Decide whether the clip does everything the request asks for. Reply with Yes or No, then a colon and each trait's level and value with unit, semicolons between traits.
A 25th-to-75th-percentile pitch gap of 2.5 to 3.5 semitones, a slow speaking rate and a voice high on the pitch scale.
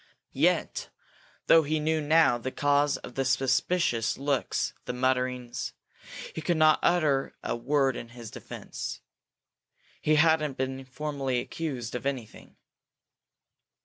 No: average, 3.2 semitones; slow, 120 wpm; low, 135 Hz